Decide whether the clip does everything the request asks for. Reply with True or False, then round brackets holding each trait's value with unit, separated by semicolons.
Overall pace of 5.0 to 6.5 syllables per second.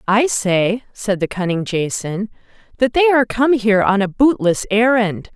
False (4.7 syllables/s)